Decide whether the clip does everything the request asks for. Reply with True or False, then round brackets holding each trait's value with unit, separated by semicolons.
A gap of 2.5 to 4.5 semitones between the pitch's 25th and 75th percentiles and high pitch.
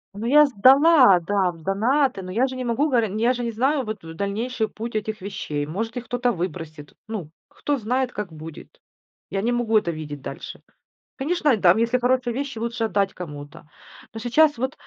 False (5.3 semitones; 225 Hz)